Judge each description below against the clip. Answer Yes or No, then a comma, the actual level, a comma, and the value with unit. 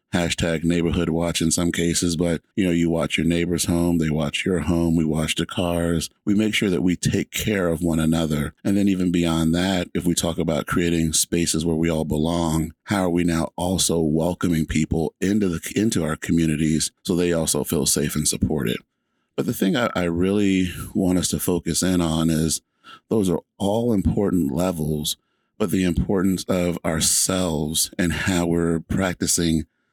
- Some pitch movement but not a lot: No, narrow, 1.9 semitones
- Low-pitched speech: Yes, very low, 85 Hz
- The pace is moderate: Yes, average, 185 wpm